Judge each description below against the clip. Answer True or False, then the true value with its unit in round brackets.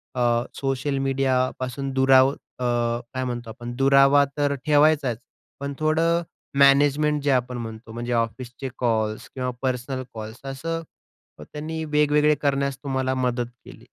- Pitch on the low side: True (130 Hz)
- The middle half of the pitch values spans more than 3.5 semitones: False (2.8 semitones)